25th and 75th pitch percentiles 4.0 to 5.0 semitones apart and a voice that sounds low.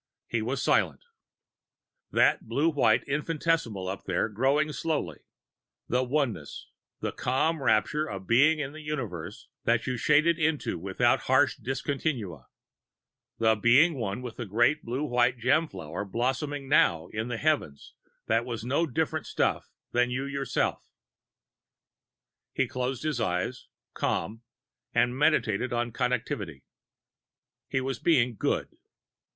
Yes: average, 4.7 semitones; low, 125 Hz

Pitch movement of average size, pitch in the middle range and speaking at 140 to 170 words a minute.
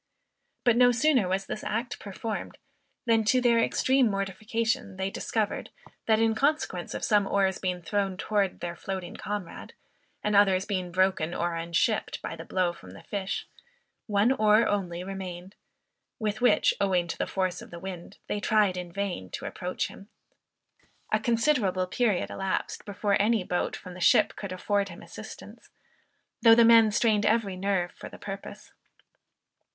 No: average, 3.1 semitones; high, 200 Hz; average, 165 wpm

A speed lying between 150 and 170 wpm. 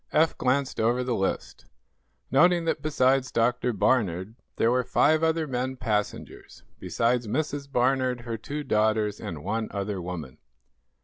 No: average, 140 wpm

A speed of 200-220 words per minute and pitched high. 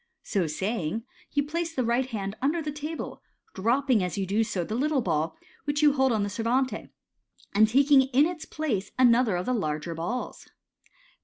No: average, 180 wpm; high, 240 Hz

